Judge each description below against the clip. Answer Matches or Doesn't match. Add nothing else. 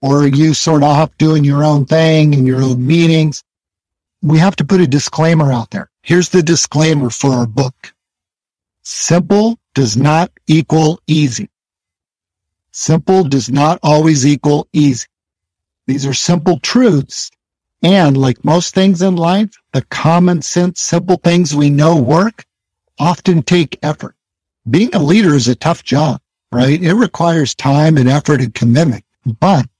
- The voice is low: Doesn't match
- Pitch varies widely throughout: Doesn't match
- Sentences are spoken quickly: Doesn't match